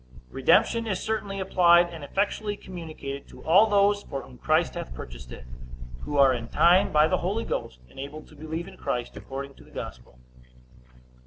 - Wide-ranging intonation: Yes, wide, 6.3 semitones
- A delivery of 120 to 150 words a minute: No, average, 175 wpm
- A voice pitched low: No, medium, 160 Hz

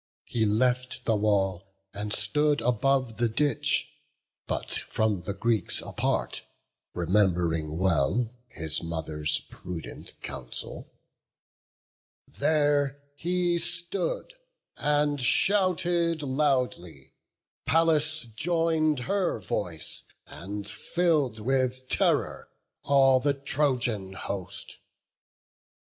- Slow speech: Yes, slow, 90 wpm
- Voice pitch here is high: No, low, 125 Hz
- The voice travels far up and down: Yes, wide, 7.3 semitones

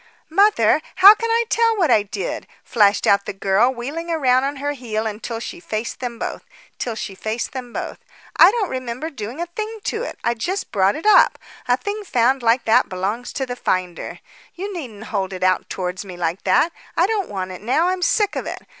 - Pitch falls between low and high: No, very high, 250 Hz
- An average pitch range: No, wide, 8.8 semitones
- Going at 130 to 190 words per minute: No, average, 200 wpm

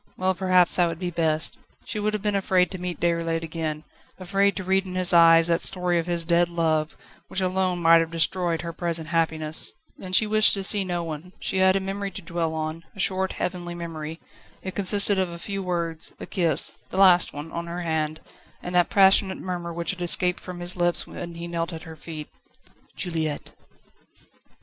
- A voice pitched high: No, medium, 175 Hz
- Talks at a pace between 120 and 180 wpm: No, fast, 205 wpm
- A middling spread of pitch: No, narrow, 2.2 semitones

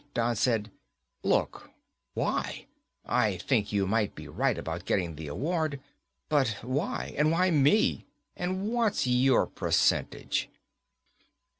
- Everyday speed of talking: No, slow, 120 wpm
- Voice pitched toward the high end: No, low, 130 Hz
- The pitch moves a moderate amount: No, wide, 7.2 semitones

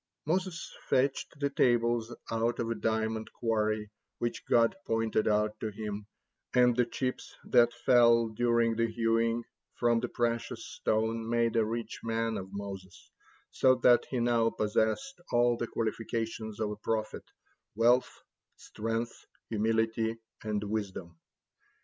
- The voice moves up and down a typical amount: No, narrow, 1.4 semitones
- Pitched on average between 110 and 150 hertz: Yes, low, 115 Hz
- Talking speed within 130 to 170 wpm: Yes, slow, 135 wpm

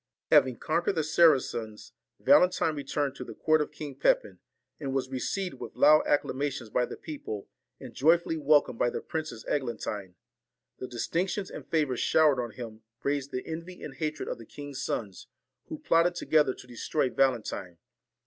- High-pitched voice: No, medium, 140 Hz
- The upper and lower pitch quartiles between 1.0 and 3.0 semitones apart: No, average, 4.0 semitones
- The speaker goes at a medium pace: Yes, average, 170 wpm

